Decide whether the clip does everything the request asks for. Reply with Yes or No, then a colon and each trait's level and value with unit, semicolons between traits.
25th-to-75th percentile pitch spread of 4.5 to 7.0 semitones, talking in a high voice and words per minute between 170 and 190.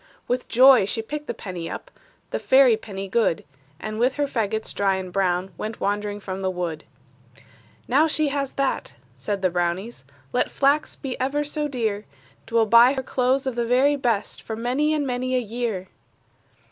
Yes: average, 5.0 semitones; high, 235 Hz; average, 185 wpm